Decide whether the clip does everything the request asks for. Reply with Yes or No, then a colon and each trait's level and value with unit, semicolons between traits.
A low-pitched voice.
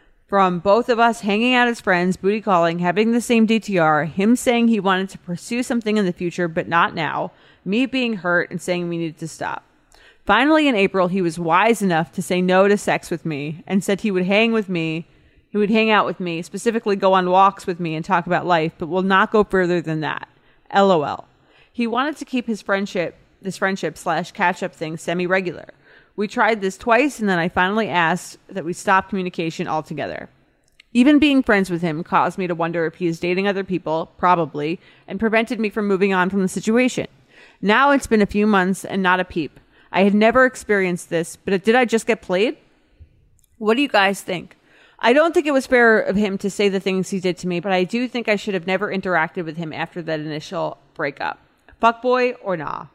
No: high, 190 Hz